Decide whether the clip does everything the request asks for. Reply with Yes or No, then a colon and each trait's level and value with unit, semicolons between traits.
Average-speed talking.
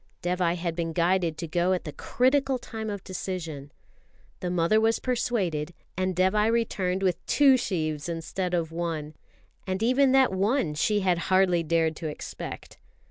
Yes: average, 160 wpm